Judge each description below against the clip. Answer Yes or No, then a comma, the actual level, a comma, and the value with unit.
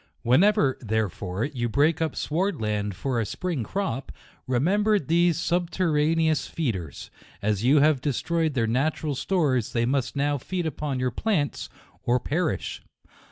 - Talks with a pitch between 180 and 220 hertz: No, medium, 145 Hz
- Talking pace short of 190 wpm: Yes, average, 140 wpm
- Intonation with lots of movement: Yes, wide, 5.7 semitones